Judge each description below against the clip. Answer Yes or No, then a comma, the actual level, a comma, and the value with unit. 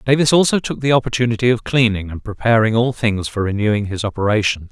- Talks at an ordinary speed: Yes, average, 190 wpm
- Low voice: Yes, low, 115 Hz